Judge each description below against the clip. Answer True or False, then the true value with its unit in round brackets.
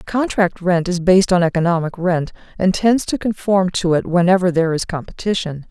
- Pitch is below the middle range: False (180 Hz)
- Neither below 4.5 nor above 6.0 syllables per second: True (5.4 syllables/s)